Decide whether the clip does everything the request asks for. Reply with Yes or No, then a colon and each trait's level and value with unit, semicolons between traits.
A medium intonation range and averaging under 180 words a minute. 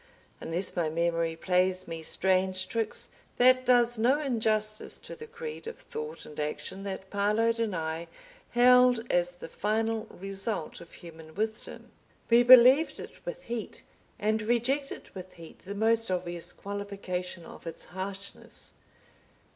Yes: average, 4.8 semitones; average, 140 wpm